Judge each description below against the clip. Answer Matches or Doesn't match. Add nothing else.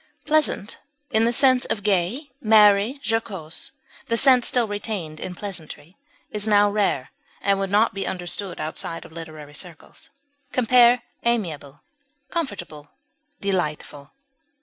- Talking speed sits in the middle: Doesn't match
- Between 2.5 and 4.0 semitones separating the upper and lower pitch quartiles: Doesn't match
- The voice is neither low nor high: Doesn't match